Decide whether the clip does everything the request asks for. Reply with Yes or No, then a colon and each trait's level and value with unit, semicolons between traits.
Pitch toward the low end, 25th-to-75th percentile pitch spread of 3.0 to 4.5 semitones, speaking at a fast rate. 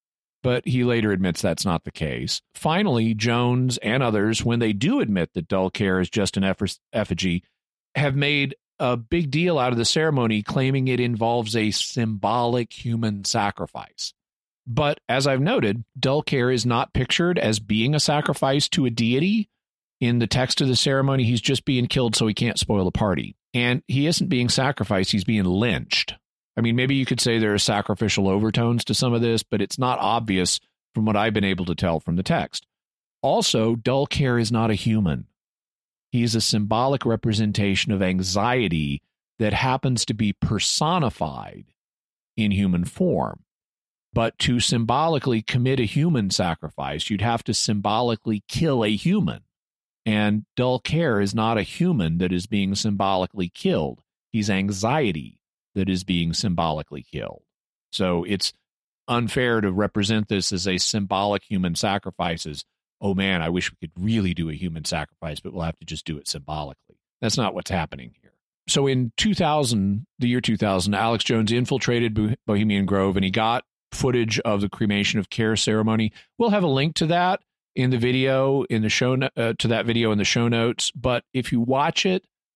No: low, 115 Hz; average, 4.1 semitones; average, 180 wpm